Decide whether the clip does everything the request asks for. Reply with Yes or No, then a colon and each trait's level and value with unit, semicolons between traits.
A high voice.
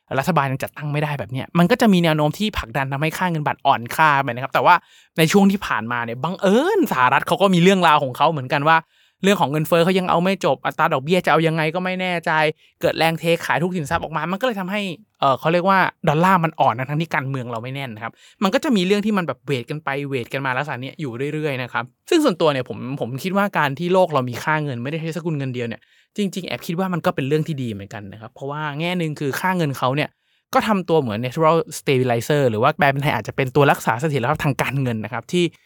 No: medium, 155 Hz